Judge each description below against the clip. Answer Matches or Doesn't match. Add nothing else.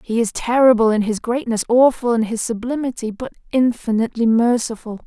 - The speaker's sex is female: Matches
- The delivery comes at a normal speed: Matches